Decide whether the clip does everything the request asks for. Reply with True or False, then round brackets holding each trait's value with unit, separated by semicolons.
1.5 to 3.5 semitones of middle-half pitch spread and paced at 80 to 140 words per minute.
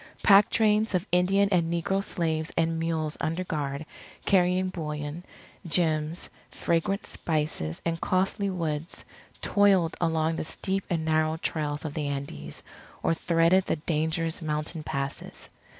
True (2.8 semitones; 135 wpm)